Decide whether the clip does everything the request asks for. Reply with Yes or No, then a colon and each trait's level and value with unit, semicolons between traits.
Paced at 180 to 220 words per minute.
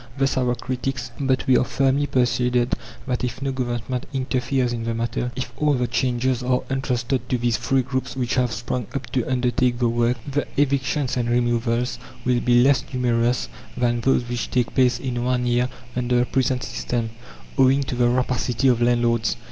Yes: average, 185 wpm